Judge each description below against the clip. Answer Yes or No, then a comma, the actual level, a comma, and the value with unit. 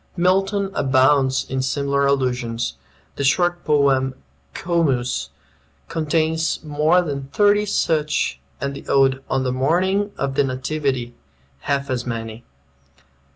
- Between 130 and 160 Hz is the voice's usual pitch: Yes, medium, 140 Hz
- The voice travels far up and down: No, average, 3.8 semitones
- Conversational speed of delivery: No, slow, 115 wpm